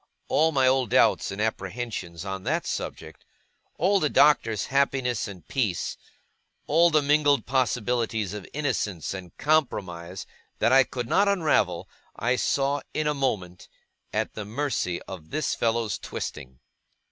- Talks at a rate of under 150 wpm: Yes, average, 140 wpm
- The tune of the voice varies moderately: No, wide, 6.7 semitones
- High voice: No, low, 120 Hz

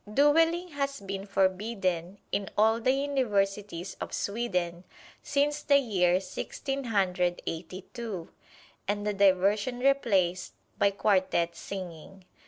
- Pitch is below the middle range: No, high, 200 Hz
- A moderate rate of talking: No, slow, 115 wpm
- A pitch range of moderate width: Yes, average, 5.0 semitones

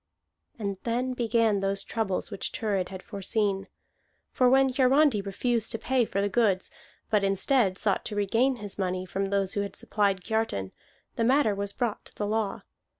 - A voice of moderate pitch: No, high, 210 Hz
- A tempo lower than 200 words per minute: Yes, average, 175 wpm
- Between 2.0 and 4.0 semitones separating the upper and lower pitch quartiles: Yes, average, 3.2 semitones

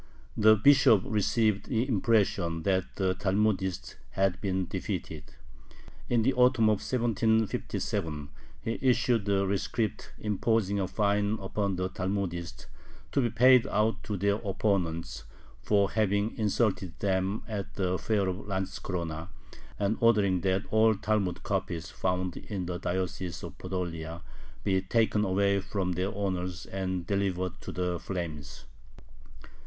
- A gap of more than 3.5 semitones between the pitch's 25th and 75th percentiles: No, average, 2.7 semitones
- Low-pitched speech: Yes, low, 100 Hz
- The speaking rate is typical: No, slow, 130 wpm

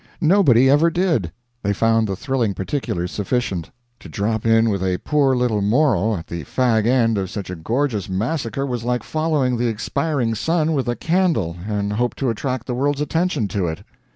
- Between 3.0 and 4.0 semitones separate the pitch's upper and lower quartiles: No, wide, 5.4 semitones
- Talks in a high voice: No, low, 120 Hz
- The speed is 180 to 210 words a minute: Yes, average, 185 wpm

